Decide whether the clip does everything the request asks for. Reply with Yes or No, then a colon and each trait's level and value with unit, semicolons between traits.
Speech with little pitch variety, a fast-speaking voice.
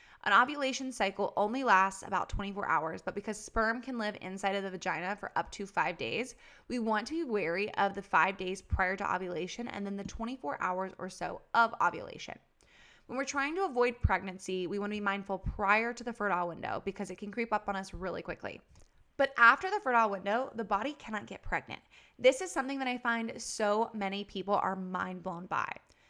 No: average, 3.6 semitones; fast, 210 wpm